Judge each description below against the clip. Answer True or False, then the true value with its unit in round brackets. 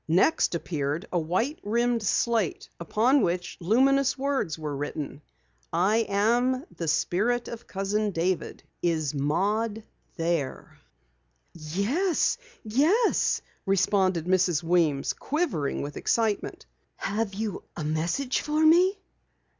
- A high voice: True (200 Hz)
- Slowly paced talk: True (110 wpm)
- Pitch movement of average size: False (6.5 semitones)